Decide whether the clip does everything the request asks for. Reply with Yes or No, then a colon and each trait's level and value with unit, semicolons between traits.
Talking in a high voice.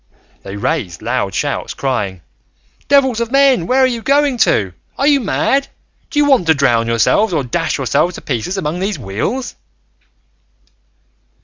No: medium, 180 Hz